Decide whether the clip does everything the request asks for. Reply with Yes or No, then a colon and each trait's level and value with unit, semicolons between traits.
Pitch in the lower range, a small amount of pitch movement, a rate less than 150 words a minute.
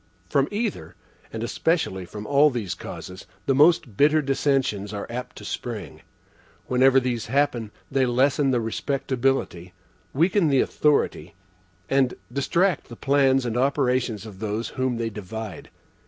No: low, 130 Hz; average, 3.8 semitones; average, 140 wpm